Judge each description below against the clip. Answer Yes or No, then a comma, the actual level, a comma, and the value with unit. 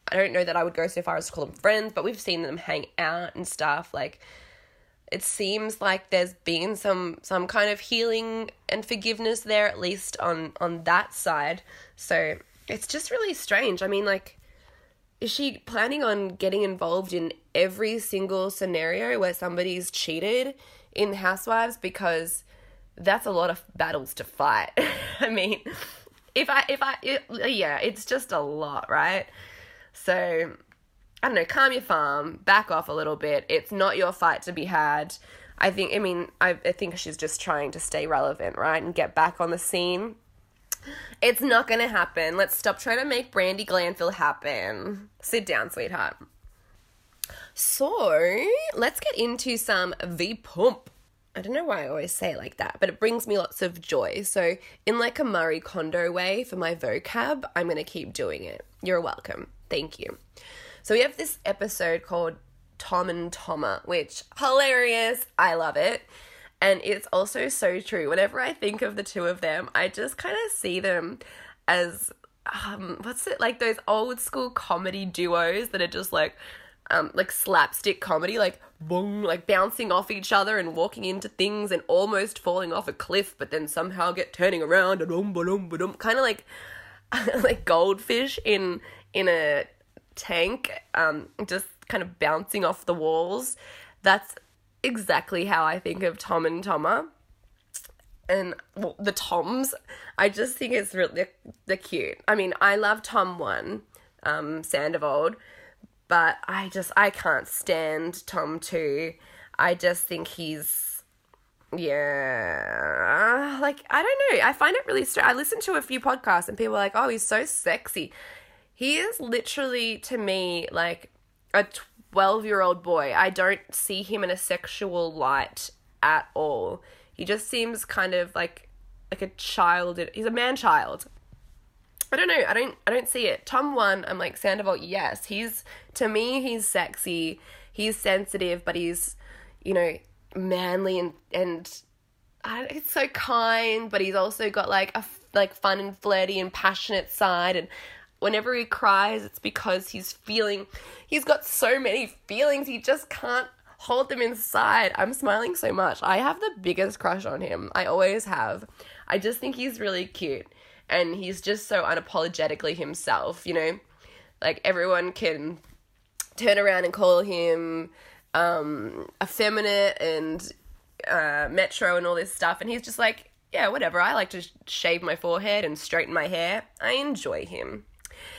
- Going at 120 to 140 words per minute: No, average, 170 wpm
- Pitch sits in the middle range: No, high, 195 Hz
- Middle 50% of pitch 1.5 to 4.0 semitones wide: No, wide, 5.4 semitones